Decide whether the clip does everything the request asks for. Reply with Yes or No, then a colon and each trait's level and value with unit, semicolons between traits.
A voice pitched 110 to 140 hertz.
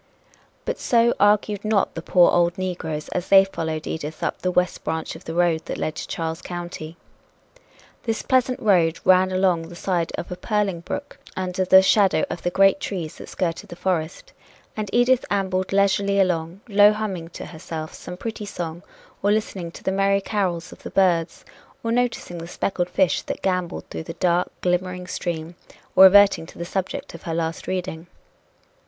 No: medium, 180 Hz